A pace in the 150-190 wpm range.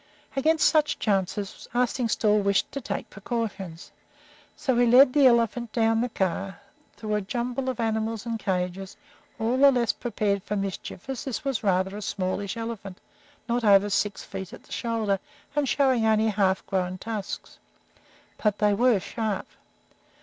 Yes: average, 155 wpm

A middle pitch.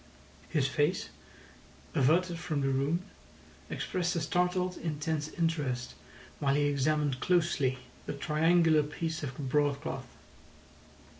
Yes: medium, 150 Hz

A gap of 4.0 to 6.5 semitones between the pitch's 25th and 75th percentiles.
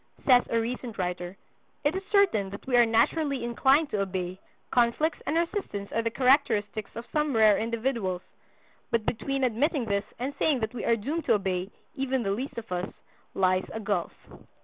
Yes: average, 5.1 semitones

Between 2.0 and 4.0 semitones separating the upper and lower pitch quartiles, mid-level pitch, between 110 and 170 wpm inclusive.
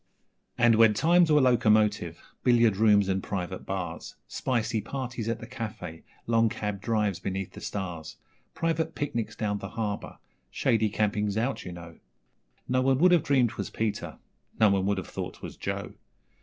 No: average, 3.6 semitones; low, 110 Hz; average, 165 wpm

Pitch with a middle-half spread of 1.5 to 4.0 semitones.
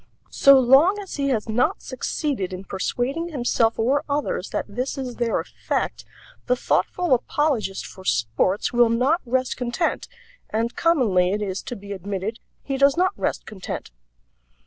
No: average, 5.3 semitones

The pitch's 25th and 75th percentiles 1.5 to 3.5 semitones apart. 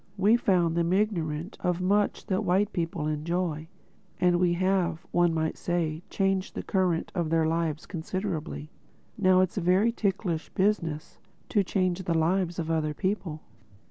Yes: average, 2.7 semitones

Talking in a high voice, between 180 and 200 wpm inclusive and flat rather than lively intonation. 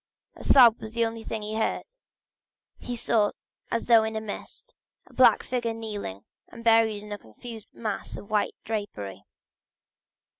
No: high, 220 Hz; average, 160 wpm; narrow, 1.8 semitones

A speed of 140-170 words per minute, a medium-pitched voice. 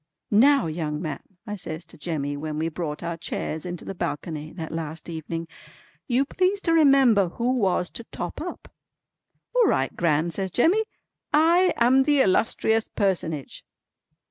Yes: average, 155 wpm; medium, 180 Hz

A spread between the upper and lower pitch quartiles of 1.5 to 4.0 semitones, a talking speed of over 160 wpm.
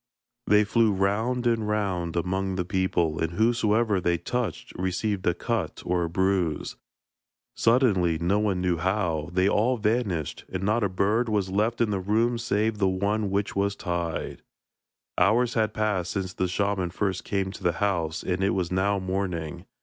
Yes: average, 2.9 semitones; average, 170 wpm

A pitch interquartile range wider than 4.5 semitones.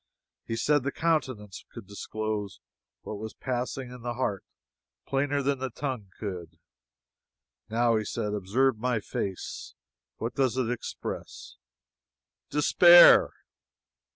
No: average, 4.1 semitones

